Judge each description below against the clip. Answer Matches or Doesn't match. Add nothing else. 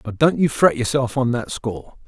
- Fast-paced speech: Matches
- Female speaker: Doesn't match